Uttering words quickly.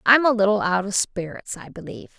Yes: fast, 220 wpm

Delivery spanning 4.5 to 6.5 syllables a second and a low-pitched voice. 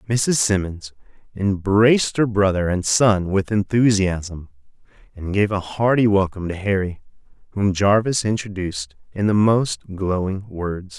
No: 4.3 syllables/s; low, 100 Hz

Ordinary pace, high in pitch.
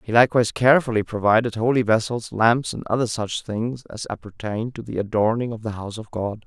No: average, 195 wpm; low, 115 Hz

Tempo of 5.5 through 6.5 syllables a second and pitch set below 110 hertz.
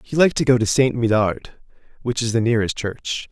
No: 5.7 syllables/s; low, 115 Hz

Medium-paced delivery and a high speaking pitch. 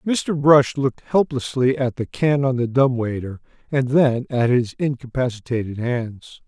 No: average, 160 wpm; low, 130 Hz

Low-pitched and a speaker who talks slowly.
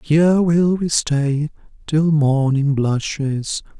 No: medium, 150 Hz; slow, 110 wpm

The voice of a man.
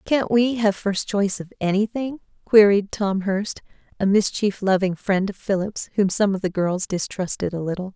No: female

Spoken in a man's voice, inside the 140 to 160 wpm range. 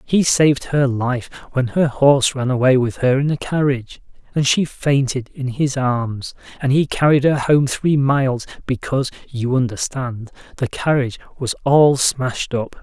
No: male; average, 170 wpm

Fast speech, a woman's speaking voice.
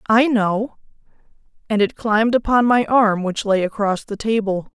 No: average, 165 wpm; female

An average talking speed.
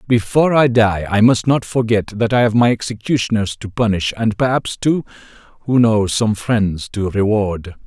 Yes: average, 175 wpm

